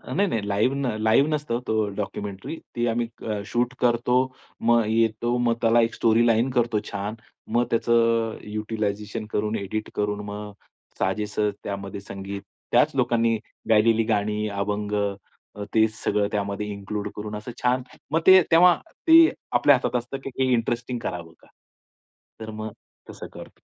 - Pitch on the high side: No, low, 110 Hz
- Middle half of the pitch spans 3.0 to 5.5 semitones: No, narrow, 2.4 semitones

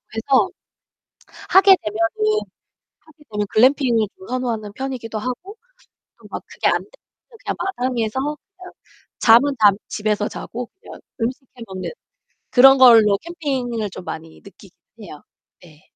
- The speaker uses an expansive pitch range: No, average, 4.5 semitones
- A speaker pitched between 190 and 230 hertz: No, high, 240 Hz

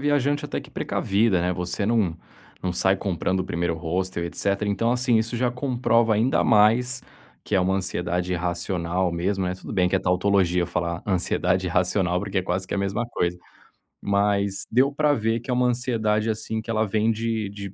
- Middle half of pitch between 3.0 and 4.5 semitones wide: Yes, average, 4.0 semitones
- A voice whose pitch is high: No, low, 100 Hz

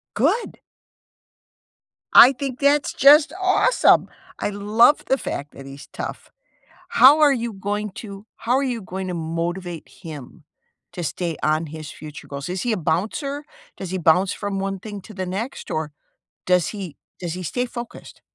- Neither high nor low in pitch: No, high, 195 Hz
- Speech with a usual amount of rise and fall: No, wide, 6.4 semitones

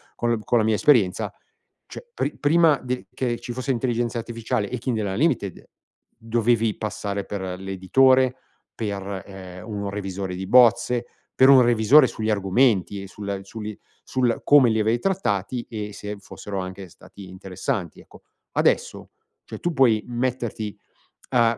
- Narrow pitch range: No, average, 3.8 semitones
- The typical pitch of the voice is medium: No, low, 110 Hz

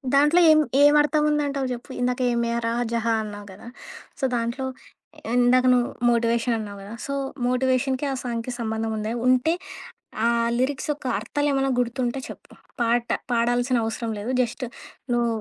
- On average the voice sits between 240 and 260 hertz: Yes, high, 245 Hz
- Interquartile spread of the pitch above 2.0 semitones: Yes, narrow, 2.4 semitones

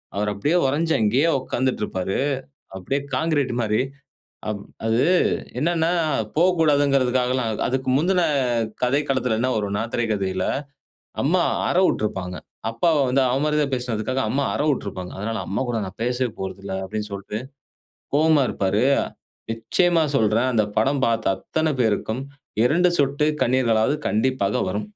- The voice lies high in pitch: No, low, 125 Hz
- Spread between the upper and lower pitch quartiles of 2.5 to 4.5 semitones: No, average, 5.1 semitones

